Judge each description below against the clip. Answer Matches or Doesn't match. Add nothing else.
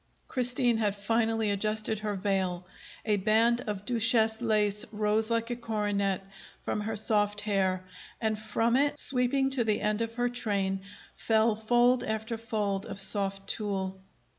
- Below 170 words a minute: Matches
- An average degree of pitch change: Doesn't match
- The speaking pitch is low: Doesn't match